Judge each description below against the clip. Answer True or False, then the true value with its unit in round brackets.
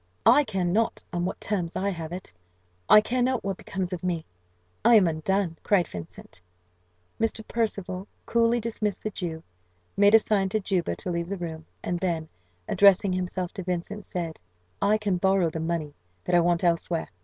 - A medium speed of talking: True (180 wpm)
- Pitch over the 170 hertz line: True (185 Hz)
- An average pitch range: True (3.3 semitones)